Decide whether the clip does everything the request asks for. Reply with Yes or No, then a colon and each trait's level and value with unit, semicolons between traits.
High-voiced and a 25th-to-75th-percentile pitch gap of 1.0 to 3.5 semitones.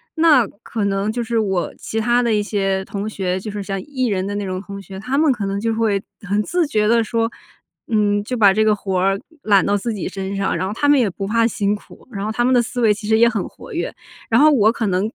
Yes: high, 210 Hz; average, 2.8 semitones